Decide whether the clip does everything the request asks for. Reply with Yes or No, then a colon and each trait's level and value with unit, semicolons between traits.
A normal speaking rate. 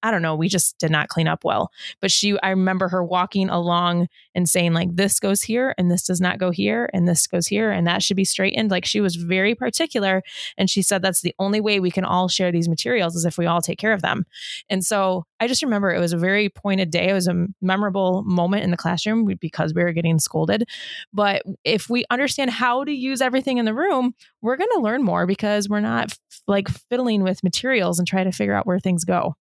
No: fast, 245 wpm